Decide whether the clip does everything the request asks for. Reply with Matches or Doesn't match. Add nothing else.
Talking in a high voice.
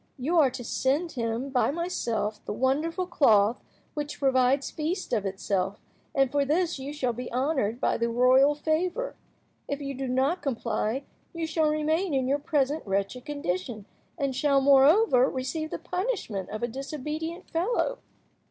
Matches